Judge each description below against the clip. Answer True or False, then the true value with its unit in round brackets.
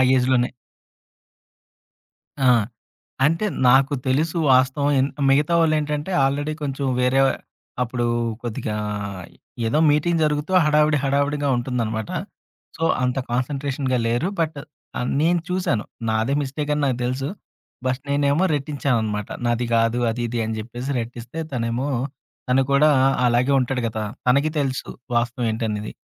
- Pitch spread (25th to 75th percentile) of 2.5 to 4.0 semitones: True (3.4 semitones)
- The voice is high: False (135 Hz)